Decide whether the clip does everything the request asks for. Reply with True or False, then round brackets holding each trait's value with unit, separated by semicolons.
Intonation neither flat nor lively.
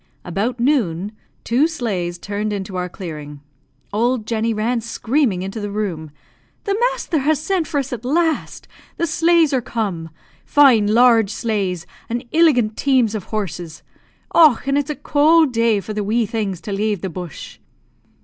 False (5.8 semitones)